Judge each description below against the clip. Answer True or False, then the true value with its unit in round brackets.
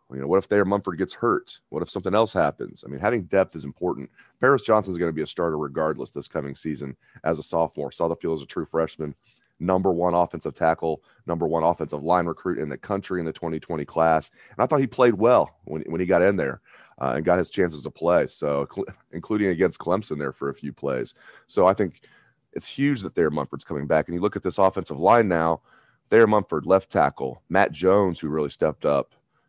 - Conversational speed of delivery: False (225 wpm)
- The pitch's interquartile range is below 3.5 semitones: False (4.0 semitones)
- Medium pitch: False (90 Hz)